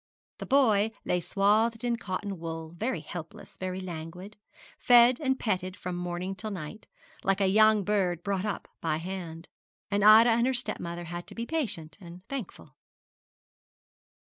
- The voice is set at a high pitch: Yes, high, 195 Hz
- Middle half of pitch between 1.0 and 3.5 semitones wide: No, average, 3.9 semitones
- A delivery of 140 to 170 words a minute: Yes, average, 155 wpm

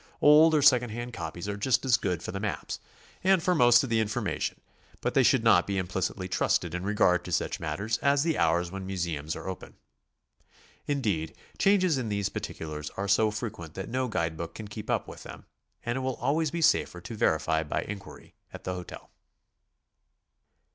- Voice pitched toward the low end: Yes, low, 105 Hz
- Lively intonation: Yes, wide, 6.3 semitones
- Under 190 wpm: No, average, 195 wpm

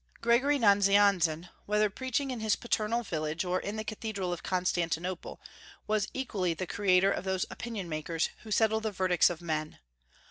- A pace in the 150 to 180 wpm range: Yes, average, 165 wpm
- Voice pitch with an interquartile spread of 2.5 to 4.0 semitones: Yes, average, 3.6 semitones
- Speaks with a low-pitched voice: No, high, 195 Hz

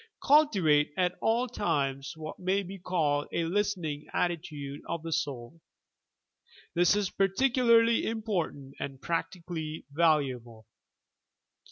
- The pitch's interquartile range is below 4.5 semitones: No, average, 5.3 semitones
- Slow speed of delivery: Yes, slow, 115 wpm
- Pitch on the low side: No, medium, 170 Hz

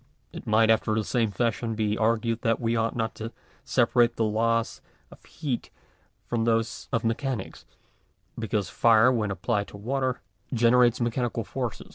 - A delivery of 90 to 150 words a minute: No, average, 160 wpm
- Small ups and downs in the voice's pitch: Yes, narrow, 1.5 semitones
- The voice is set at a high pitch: No, low, 115 Hz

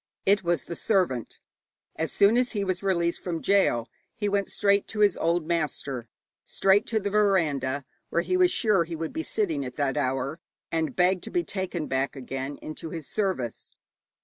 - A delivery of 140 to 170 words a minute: No, average, 185 wpm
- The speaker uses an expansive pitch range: Yes, wide, 5.7 semitones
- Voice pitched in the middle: Yes, medium, 170 Hz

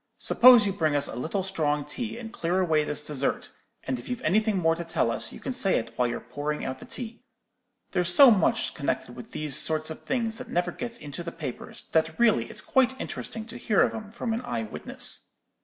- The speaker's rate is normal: No, fast, 225 wpm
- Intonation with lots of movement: Yes, wide, 7.2 semitones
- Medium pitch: Yes, medium, 175 Hz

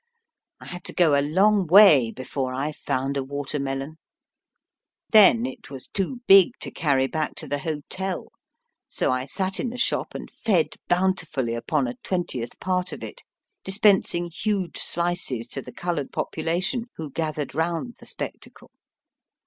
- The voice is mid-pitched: Yes, medium, 165 Hz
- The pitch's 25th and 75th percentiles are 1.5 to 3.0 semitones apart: No, wide, 5.4 semitones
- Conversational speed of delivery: Yes, average, 160 wpm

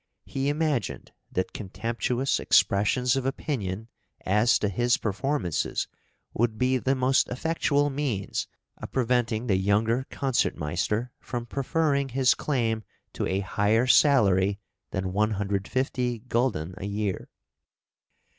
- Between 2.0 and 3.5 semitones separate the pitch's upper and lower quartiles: No, average, 4.6 semitones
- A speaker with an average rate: No, slow, 115 wpm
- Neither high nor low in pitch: No, low, 120 Hz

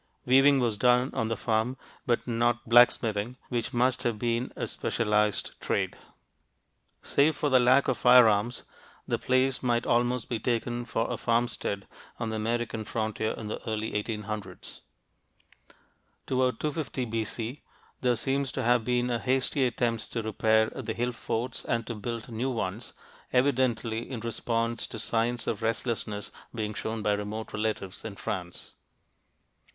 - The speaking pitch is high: No, low, 115 Hz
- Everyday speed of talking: Yes, average, 150 wpm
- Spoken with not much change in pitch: Yes, narrow, 2.1 semitones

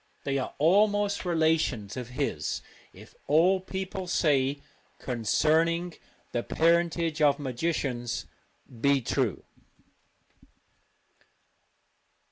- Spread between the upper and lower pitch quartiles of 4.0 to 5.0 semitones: Yes, average, 4.5 semitones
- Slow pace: Yes, slow, 85 wpm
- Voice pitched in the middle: Yes, medium, 155 Hz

